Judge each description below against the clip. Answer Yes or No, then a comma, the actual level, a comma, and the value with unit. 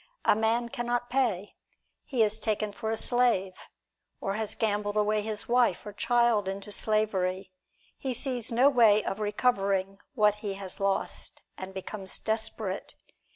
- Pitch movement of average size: Yes, average, 3.0 semitones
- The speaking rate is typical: Yes, average, 155 wpm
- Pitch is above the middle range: Yes, high, 215 Hz